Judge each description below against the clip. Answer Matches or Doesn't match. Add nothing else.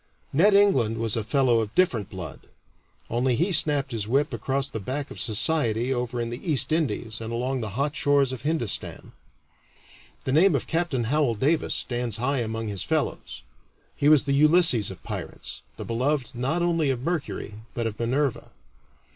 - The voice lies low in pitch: Matches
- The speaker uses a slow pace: Doesn't match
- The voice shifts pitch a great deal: Doesn't match